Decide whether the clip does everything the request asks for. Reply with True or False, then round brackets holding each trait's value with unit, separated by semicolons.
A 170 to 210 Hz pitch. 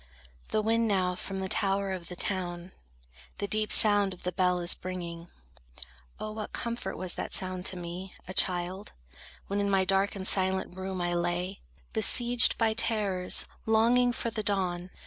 True (190 Hz)